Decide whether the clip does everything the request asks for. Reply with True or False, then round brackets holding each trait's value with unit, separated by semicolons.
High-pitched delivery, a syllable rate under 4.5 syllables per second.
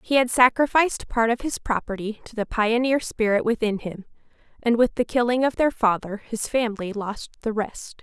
False (230 Hz; 5.2 syllables/s)